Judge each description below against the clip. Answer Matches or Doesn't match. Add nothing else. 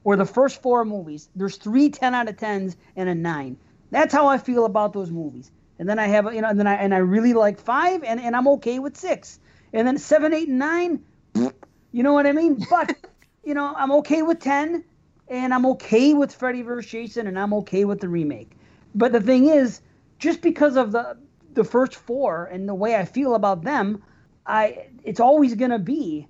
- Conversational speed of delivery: Doesn't match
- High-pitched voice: Matches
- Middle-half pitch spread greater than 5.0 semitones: Matches